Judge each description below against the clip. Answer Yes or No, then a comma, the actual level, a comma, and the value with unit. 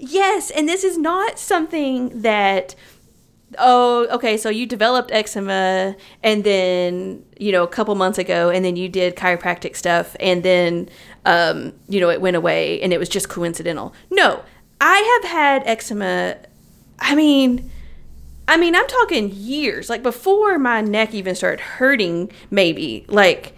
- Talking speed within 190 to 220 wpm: No, average, 155 wpm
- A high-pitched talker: Yes, high, 215 Hz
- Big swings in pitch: Yes, wide, 7.3 semitones